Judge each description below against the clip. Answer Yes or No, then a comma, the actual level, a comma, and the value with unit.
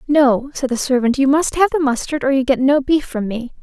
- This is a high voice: Yes, very high, 270 Hz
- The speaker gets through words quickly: Yes, fast, 265 wpm